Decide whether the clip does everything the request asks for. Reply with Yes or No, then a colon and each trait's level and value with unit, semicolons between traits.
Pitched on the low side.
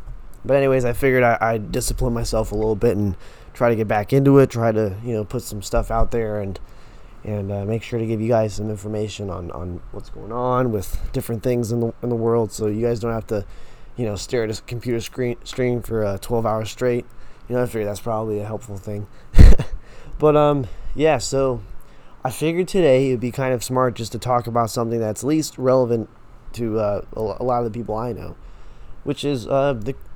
Yes: low, 115 Hz